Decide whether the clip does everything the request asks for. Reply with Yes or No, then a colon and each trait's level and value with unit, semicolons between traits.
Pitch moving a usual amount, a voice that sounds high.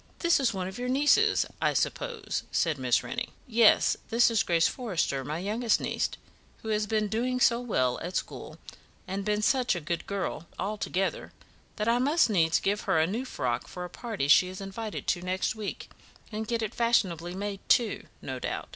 Yes: average, 4.6 semitones; high, 210 Hz